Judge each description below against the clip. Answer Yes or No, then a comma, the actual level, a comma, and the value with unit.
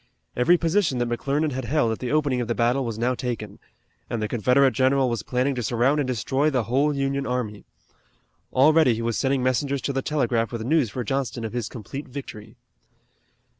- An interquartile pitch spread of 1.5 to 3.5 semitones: Yes, average, 2.8 semitones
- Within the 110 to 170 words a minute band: No, average, 200 wpm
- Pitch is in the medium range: No, low, 125 Hz